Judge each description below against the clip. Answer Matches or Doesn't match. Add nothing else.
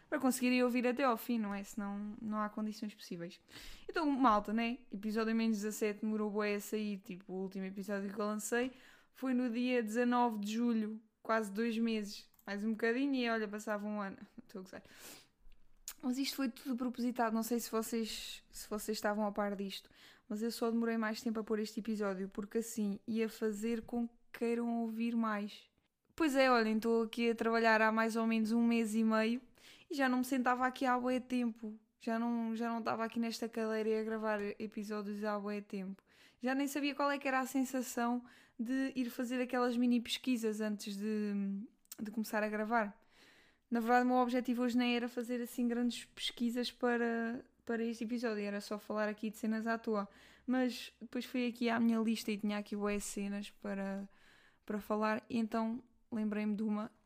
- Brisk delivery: Matches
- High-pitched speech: Matches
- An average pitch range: Doesn't match